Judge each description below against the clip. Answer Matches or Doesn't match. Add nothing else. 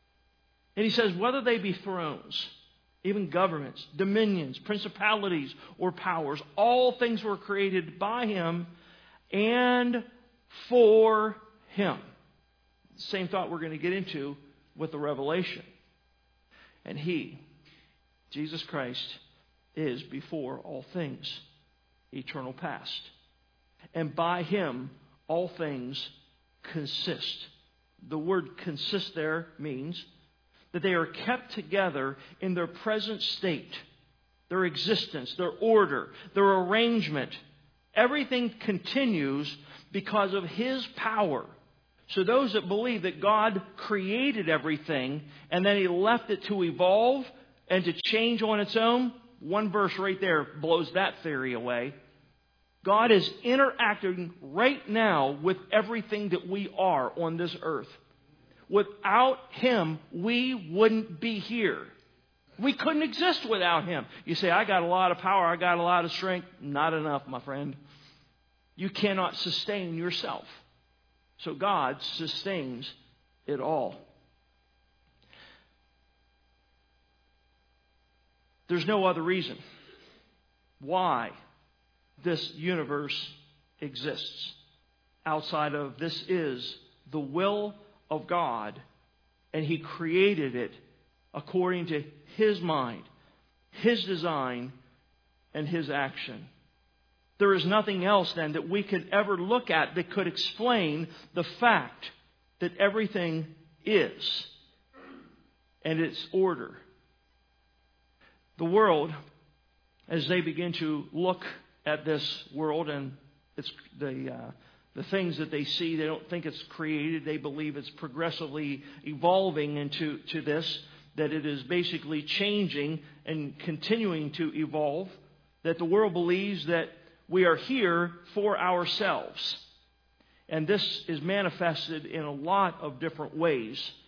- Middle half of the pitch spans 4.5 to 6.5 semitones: Matches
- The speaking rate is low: Matches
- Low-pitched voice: Doesn't match